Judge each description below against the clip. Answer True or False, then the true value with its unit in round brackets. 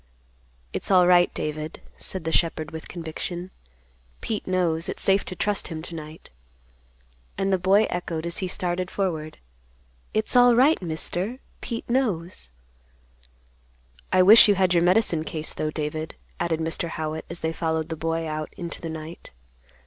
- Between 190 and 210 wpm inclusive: False (160 wpm)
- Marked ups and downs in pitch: False (2.8 semitones)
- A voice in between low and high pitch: True (170 Hz)